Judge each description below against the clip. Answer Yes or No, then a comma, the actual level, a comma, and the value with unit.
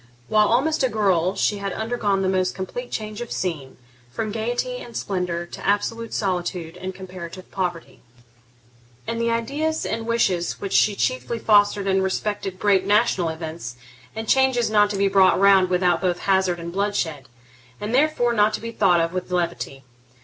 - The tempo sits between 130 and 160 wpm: No, average, 170 wpm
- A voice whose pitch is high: Yes, high, 195 Hz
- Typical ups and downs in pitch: Yes, average, 3.7 semitones